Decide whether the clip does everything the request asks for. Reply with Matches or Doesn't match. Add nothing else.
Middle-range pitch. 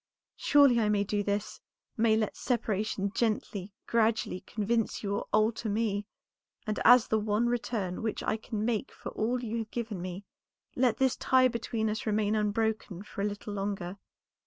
Doesn't match